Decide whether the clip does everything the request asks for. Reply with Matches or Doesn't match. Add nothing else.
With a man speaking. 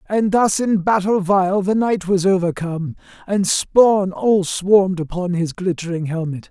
Matches